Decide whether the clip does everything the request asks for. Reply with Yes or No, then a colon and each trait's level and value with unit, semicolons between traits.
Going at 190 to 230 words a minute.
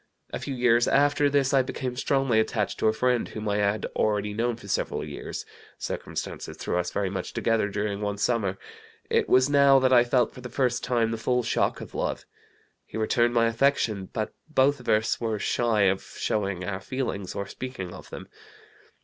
Yes: average, 195 wpm